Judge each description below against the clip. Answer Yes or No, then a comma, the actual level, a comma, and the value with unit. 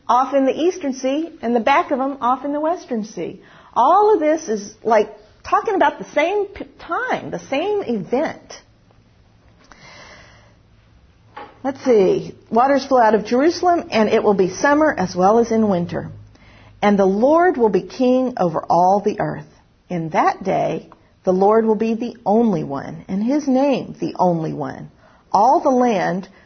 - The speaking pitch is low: No, high, 240 Hz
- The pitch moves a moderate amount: No, wide, 5.8 semitones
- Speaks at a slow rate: No, average, 170 wpm